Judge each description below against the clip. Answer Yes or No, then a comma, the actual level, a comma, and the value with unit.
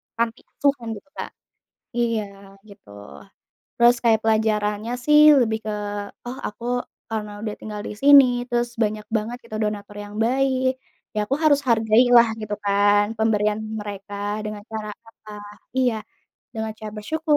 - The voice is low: No, high, 220 Hz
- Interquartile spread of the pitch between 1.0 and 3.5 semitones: Yes, narrow, 2.4 semitones